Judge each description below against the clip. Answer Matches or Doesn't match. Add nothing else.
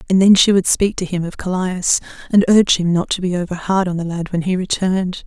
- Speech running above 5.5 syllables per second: Matches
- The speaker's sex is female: Matches